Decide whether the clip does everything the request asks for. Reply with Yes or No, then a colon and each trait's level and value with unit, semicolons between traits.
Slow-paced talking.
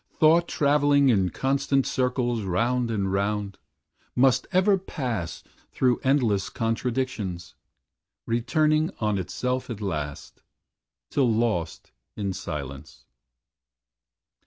Yes: slow, 95 wpm